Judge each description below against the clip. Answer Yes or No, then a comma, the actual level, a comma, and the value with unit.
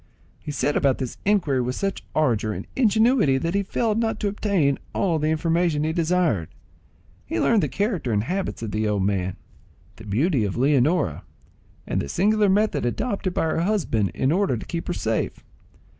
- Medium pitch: Yes, medium, 160 Hz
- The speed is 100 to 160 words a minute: No, average, 185 wpm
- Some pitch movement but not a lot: No, wide, 8.5 semitones